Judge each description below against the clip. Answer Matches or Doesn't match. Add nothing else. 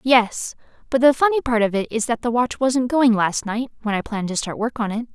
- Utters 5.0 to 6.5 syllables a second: Matches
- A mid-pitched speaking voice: Doesn't match